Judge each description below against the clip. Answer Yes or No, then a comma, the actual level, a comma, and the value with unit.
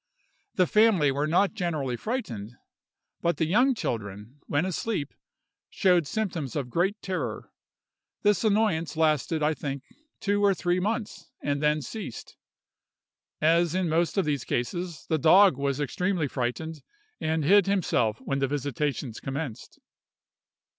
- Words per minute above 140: No, slow, 135 wpm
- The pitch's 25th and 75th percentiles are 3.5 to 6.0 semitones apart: Yes, average, 5.2 semitones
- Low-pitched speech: No, medium, 160 Hz